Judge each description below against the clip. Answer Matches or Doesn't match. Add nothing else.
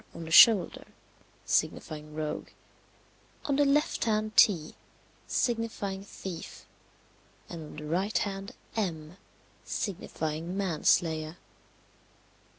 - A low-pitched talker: Doesn't match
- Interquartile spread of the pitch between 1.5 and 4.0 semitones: Doesn't match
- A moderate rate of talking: Doesn't match